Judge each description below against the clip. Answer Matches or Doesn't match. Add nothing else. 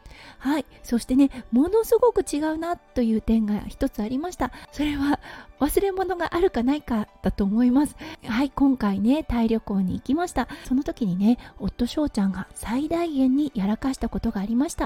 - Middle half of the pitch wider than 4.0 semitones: Matches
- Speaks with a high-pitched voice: Matches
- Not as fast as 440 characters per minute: Matches